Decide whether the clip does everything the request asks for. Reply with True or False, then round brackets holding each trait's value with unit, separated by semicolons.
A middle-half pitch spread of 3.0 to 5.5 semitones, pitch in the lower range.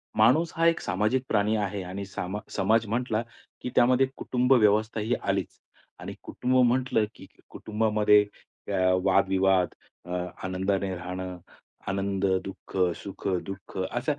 True (3.6 semitones; 105 Hz)